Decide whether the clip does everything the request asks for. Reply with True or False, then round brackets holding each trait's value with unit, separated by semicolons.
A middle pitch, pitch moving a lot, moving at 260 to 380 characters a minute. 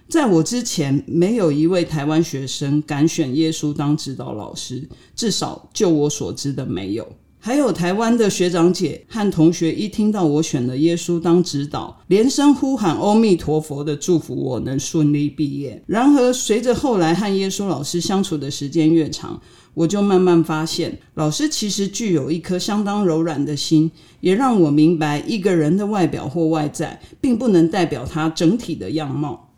False (165 Hz; 4.3 semitones; 270 characters per minute)